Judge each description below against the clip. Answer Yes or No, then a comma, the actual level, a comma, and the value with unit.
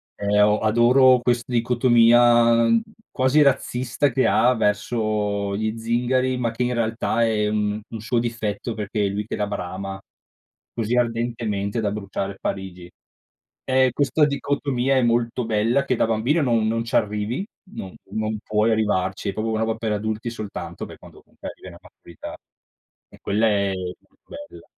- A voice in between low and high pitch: No, low, 115 Hz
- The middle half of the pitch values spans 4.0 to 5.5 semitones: No, narrow, 2.6 semitones